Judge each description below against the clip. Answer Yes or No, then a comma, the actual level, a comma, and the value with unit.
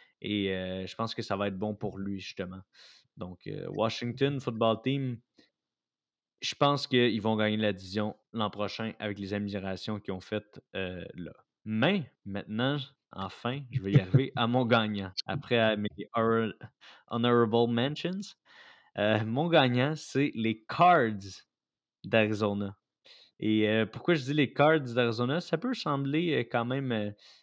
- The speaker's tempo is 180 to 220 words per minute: No, average, 155 wpm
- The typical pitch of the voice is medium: No, low, 115 Hz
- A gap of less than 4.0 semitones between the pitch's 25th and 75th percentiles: No, average, 4.5 semitones